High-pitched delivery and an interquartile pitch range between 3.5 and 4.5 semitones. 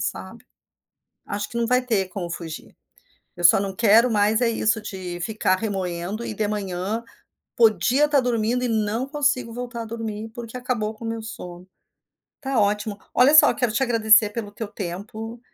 No: high, 220 Hz; average, 2.7 semitones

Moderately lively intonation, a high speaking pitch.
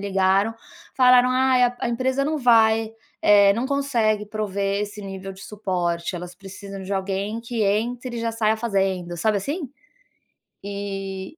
Yes: average, 3.6 semitones; high, 210 Hz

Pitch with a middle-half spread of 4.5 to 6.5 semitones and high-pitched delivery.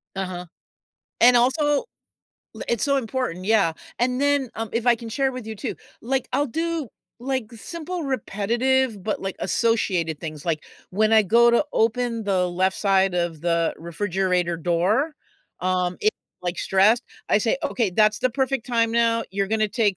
Yes: average, 5.2 semitones; high, 220 Hz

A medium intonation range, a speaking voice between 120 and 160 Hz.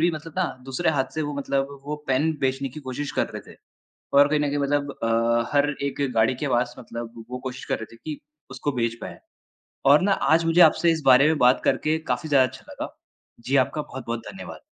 Yes: average, 3.1 semitones; medium, 140 Hz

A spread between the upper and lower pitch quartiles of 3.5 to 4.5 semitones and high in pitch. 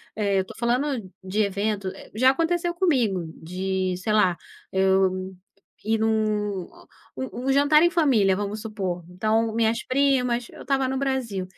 No: wide, 5.4 semitones; high, 215 Hz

